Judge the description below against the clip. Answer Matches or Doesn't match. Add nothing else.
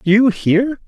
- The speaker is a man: Matches